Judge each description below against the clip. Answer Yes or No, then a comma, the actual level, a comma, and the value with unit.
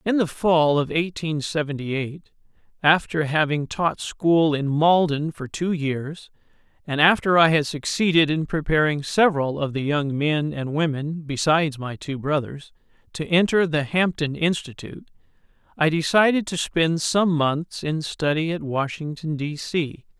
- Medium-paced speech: Yes, average, 150 wpm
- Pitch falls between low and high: Yes, medium, 155 Hz